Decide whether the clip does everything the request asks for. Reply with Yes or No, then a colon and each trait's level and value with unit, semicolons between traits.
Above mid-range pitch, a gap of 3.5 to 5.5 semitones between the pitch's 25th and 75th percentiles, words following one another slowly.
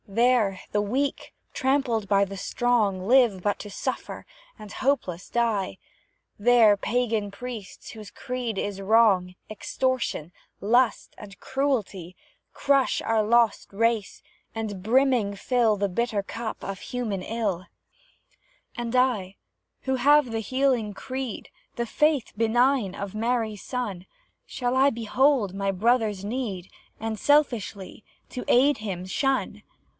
Yes: high, 225 Hz; average, 3.9 semitones; slow, 125 wpm